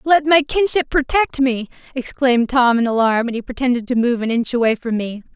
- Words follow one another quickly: Yes, fast, 215 wpm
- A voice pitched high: Yes, very high, 255 Hz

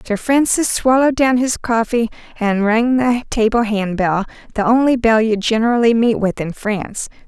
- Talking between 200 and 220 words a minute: No, average, 165 wpm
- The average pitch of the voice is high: Yes, high, 230 Hz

